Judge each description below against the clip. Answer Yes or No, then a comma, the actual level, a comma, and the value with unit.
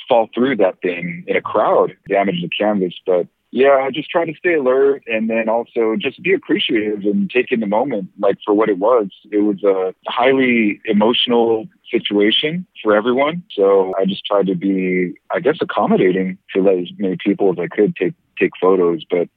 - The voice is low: Yes, low, 105 Hz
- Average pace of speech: Yes, average, 195 wpm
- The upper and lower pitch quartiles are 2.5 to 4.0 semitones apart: No, average, 4.5 semitones